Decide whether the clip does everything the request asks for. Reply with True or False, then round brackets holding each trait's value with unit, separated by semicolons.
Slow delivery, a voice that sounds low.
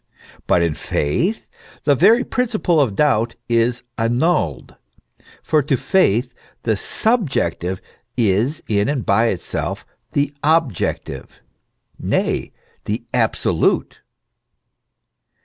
True (95 wpm; 125 Hz)